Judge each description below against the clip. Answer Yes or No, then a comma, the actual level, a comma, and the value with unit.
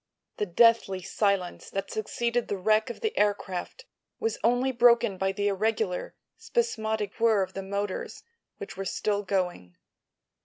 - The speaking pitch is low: No, high, 205 Hz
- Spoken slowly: No, average, 145 wpm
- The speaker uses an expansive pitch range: No, average, 3.4 semitones